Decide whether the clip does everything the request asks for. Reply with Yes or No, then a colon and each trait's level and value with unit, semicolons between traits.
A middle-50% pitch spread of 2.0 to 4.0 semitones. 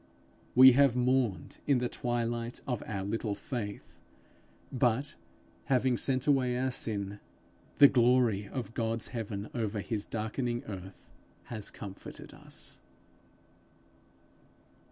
Yes: average, 3.1 semitones